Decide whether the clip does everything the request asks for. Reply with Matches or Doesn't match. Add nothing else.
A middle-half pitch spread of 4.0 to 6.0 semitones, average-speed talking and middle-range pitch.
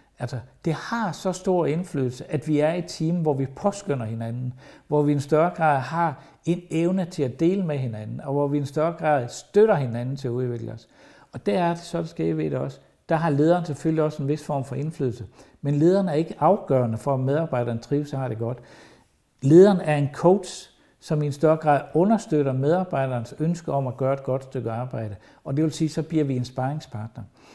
Doesn't match